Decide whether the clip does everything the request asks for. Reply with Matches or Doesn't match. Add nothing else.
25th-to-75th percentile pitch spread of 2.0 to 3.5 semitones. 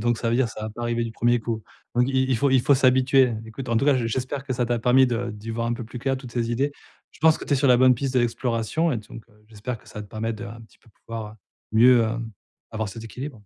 Matches